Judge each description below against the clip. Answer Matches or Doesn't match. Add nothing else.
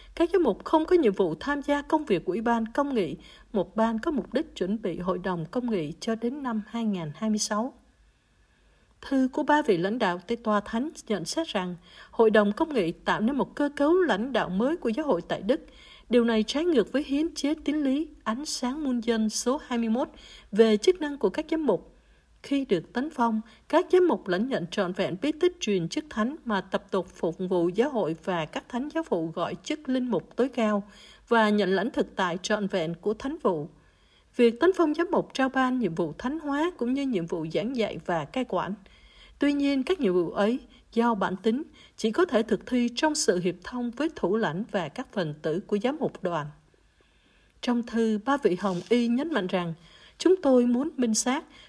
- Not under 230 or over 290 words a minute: Doesn't match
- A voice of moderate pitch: Doesn't match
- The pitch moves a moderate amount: Doesn't match